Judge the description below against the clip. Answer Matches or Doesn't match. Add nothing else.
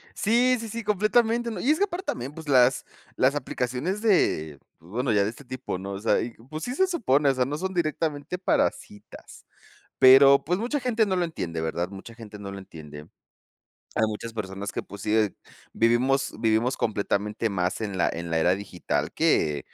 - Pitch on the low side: Matches